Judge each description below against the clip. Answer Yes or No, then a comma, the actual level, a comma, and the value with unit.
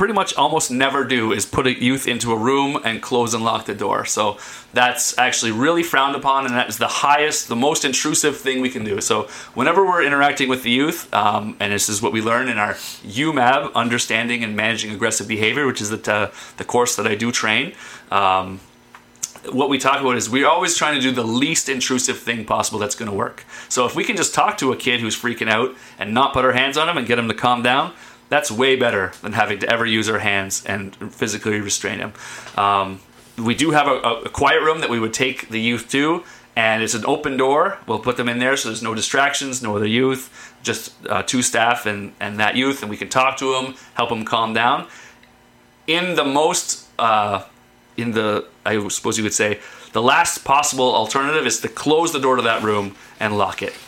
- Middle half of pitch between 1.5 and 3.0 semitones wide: No, average, 3.6 semitones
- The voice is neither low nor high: No, low, 120 Hz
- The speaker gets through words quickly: Yes, fast, 225 wpm